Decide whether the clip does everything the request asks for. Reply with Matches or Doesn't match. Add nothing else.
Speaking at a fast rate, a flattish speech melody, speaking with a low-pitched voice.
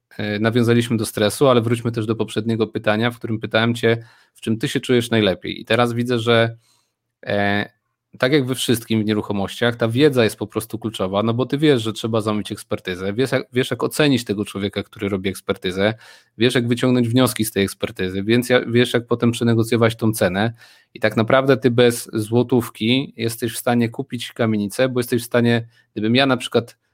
Matches